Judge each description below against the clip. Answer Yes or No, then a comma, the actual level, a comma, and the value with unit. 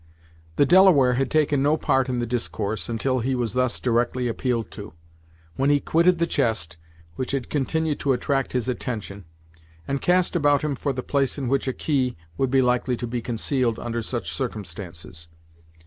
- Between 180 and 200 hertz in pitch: No, low, 125 Hz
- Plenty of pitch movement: No, average, 3.1 semitones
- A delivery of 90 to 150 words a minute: No, average, 180 wpm